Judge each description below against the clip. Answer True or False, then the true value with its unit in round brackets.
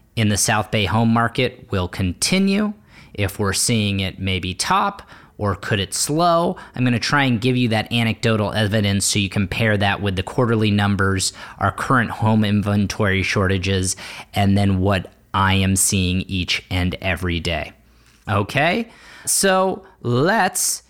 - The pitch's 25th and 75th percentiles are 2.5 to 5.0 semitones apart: True (3.5 semitones)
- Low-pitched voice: True (105 Hz)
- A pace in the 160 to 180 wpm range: False (150 wpm)